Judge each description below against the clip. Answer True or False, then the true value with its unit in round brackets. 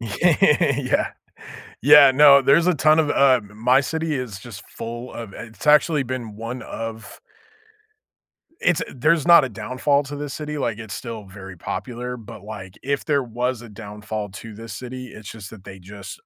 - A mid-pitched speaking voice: False (125 Hz)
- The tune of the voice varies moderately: True (4.7 semitones)